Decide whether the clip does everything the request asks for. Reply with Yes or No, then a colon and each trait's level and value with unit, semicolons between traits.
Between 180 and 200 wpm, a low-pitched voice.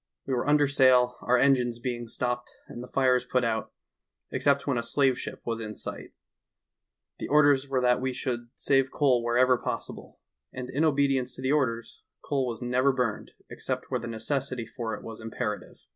Yes: average, 185 wpm; low, 125 Hz